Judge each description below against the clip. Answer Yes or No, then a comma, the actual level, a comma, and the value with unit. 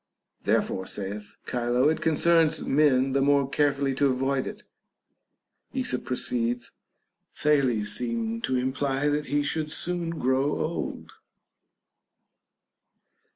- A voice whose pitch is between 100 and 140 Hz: Yes, low, 135 Hz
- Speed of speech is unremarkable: No, slow, 110 wpm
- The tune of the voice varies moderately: Yes, average, 3.2 semitones